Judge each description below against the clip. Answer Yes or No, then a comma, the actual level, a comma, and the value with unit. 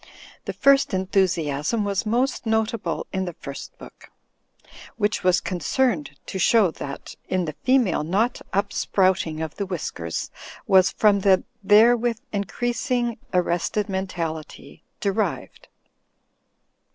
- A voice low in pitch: No, high, 195 Hz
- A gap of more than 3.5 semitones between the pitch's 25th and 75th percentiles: Yes, average, 4.1 semitones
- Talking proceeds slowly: Yes, slow, 115 wpm